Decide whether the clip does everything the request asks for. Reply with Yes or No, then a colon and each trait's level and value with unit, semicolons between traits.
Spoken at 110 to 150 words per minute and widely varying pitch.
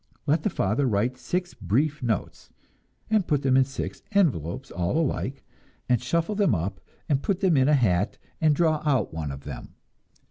No: average, 180 wpm; wide, 7.0 semitones